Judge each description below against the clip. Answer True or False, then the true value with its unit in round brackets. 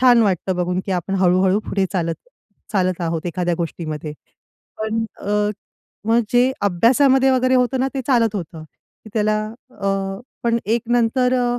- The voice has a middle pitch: False (205 Hz)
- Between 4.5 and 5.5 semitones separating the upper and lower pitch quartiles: True (5.2 semitones)